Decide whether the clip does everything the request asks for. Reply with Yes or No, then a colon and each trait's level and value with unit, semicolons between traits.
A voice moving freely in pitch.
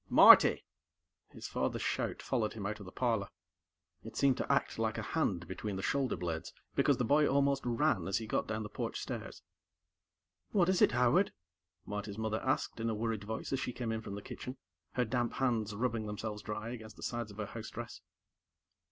No: average, 3.1 semitones